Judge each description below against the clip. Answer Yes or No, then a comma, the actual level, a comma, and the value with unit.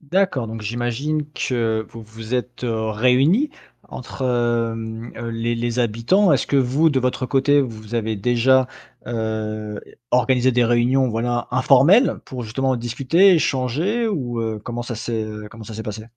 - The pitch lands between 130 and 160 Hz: No, low, 120 Hz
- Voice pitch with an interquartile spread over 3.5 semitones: No, average, 2.8 semitones